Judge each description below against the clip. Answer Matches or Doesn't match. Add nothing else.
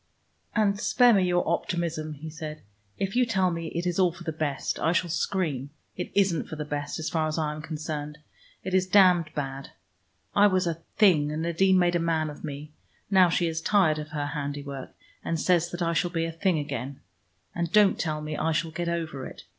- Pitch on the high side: Doesn't match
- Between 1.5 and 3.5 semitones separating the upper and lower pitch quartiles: Matches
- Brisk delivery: Matches